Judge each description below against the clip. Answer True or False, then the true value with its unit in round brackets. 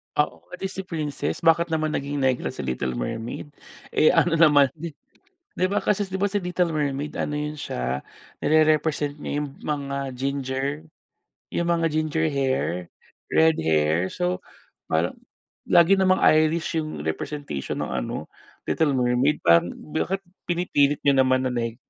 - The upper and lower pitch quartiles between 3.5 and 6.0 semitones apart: True (4.0 semitones)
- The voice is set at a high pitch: False (145 Hz)